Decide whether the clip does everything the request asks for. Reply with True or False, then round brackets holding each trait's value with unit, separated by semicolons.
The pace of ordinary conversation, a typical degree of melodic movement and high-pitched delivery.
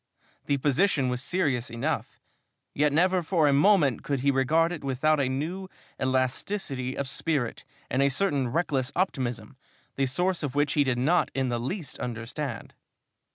False (160 wpm; 4.1 semitones; 140 Hz)